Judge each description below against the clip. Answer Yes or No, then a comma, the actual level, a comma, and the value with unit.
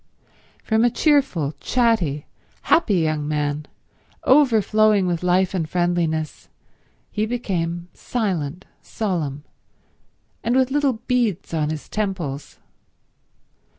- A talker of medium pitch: Yes, medium, 180 Hz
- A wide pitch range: Yes, wide, 6.2 semitones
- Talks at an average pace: No, slow, 100 wpm